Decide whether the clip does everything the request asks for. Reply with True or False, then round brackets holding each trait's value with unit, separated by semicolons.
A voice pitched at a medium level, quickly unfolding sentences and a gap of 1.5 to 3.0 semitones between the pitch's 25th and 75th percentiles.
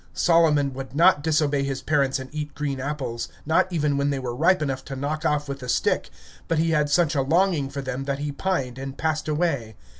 True (145 Hz; 220 wpm; 2.5 semitones)